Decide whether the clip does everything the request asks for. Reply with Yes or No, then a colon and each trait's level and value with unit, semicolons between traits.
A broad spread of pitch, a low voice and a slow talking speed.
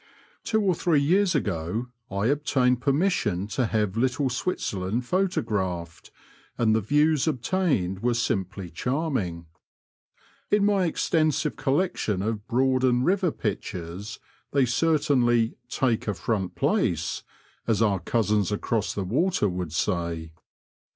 Yes: wide, 6.8 semitones; low, 120 Hz; slow, 125 wpm